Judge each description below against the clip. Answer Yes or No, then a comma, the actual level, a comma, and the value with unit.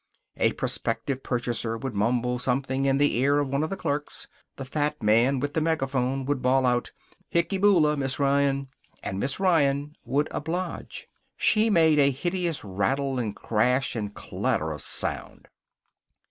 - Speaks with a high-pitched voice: No, low, 135 Hz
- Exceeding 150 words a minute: Yes, average, 160 wpm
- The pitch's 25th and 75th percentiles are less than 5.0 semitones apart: Yes, average, 3.2 semitones